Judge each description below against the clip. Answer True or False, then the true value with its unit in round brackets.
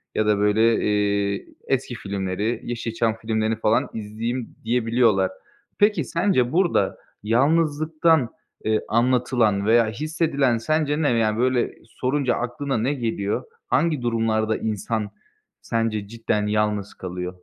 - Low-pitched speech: True (115 Hz)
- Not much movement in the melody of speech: False (3.3 semitones)